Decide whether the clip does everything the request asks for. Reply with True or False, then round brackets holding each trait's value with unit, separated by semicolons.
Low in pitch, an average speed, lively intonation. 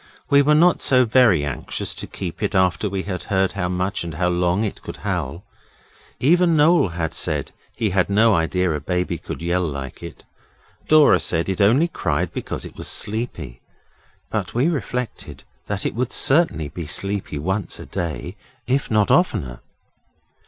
True (95 Hz; 175 wpm; 6.5 semitones)